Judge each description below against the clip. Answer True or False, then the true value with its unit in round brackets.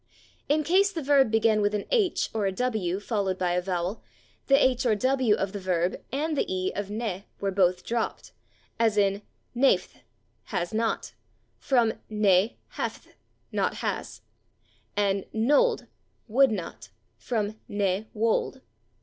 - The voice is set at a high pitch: True (215 Hz)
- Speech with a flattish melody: False (4.6 semitones)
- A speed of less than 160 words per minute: True (150 wpm)